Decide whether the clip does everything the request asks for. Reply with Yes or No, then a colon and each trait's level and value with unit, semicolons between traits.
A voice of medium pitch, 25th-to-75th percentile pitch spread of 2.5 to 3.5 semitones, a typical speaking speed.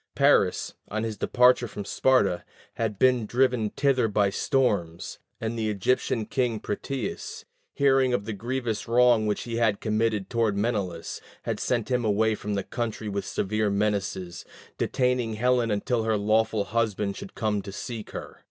No: low, 110 Hz; average, 3.0 semitones; average, 160 wpm